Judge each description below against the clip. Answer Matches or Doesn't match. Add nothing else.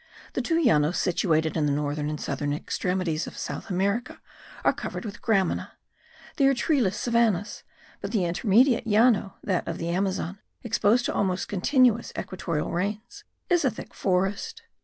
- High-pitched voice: Matches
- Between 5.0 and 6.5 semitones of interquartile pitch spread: Matches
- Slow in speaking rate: Doesn't match